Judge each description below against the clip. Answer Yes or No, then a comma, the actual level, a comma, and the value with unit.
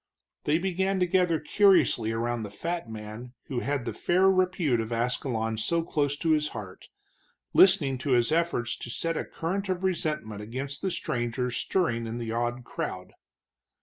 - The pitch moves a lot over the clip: Yes, wide, 6.7 semitones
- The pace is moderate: Yes, average, 170 wpm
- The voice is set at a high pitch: No, medium, 140 Hz